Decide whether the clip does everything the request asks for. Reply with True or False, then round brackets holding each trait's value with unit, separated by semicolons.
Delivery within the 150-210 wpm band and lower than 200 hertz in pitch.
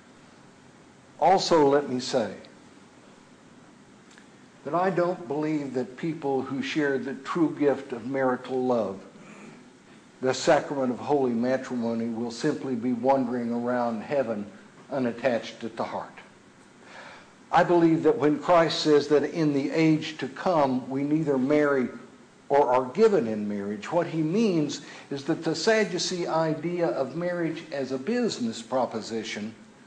False (135 wpm; 140 Hz)